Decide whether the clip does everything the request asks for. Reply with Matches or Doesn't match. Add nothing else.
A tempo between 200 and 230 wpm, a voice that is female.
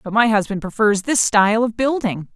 Matches